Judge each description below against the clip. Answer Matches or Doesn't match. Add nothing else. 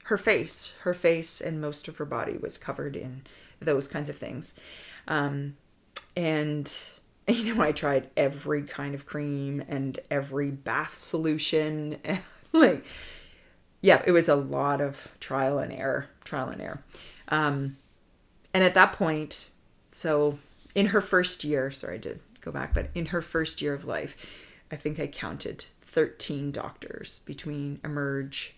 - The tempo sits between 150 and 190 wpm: Matches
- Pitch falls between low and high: Matches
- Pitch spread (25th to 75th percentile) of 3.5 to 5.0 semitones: Doesn't match